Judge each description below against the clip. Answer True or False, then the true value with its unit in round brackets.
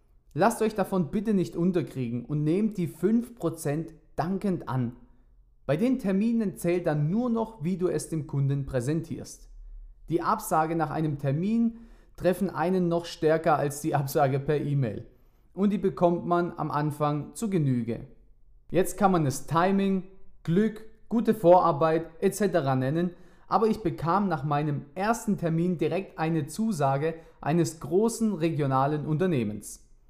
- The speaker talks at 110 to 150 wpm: True (140 wpm)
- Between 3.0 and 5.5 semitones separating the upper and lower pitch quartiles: True (4.7 semitones)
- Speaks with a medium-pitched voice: True (165 Hz)